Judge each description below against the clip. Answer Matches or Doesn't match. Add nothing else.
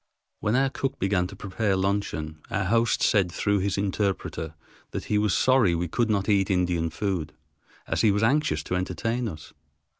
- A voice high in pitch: Doesn't match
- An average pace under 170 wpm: Doesn't match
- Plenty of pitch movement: Doesn't match